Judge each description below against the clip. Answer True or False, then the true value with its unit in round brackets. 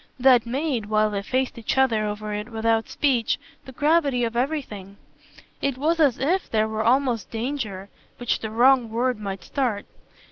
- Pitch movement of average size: True (3.6 semitones)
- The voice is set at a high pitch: True (235 Hz)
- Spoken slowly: False (170 wpm)